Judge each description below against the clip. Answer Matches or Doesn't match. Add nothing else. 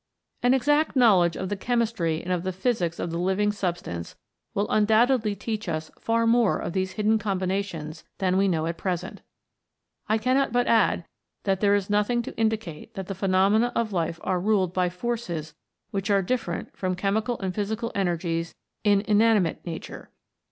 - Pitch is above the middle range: Matches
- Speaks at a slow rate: Doesn't match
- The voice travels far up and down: Doesn't match